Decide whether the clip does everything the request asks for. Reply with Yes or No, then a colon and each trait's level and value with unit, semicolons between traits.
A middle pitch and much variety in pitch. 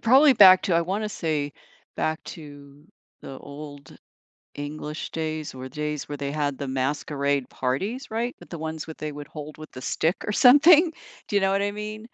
Yes: medium, 155 Hz; wide, 6.0 semitones